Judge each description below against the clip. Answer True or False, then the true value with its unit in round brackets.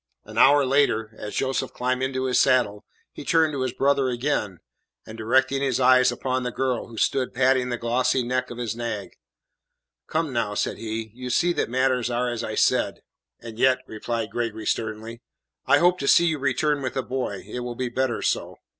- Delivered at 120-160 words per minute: False (200 wpm)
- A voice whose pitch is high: False (125 Hz)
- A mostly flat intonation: True (2.3 semitones)